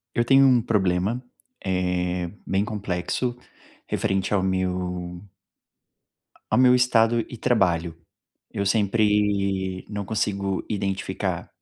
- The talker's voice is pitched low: Yes, low, 100 Hz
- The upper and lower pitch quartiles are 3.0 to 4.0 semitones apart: Yes, average, 3.3 semitones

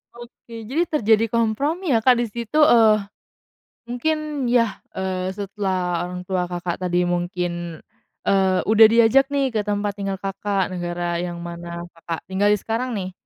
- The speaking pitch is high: Yes, high, 200 Hz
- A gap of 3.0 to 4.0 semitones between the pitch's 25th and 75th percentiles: No, average, 4.8 semitones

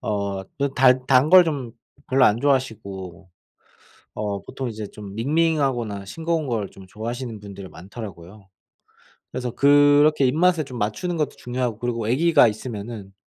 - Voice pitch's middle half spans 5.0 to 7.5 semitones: Yes, wide, 5.4 semitones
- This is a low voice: Yes, low, 120 Hz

